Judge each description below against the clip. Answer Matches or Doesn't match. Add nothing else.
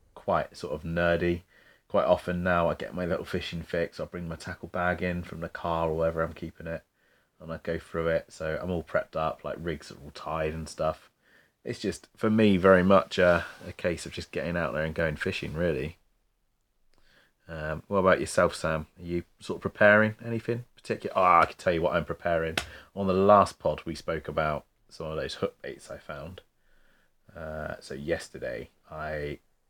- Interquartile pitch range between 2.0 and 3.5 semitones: Matches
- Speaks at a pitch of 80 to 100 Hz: Matches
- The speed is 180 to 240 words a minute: Matches